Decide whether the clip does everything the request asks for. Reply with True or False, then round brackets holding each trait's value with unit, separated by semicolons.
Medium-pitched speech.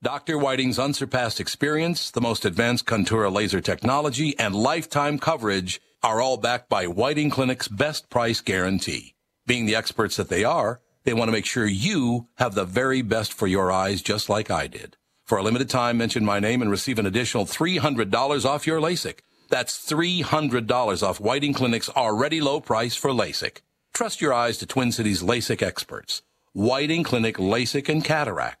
False (125 Hz)